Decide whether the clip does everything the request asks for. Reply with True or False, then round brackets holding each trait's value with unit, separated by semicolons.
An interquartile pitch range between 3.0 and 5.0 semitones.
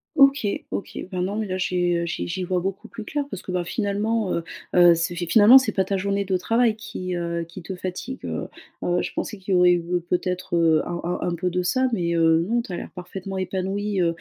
False (2.6 semitones)